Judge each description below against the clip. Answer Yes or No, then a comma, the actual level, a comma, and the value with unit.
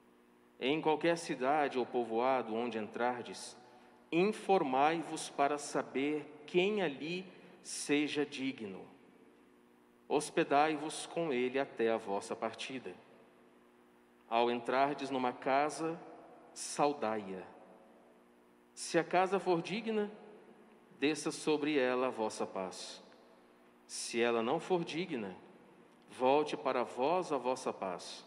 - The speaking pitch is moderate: No, low, 130 Hz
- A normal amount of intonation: No, wide, 6.3 semitones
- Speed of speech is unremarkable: No, slow, 100 wpm